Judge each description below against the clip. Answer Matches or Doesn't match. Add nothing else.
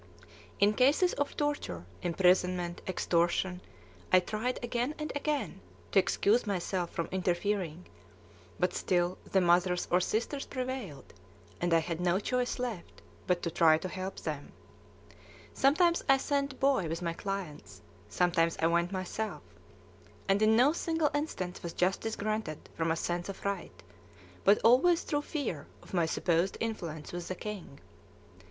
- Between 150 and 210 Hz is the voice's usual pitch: Matches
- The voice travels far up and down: Matches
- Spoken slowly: Doesn't match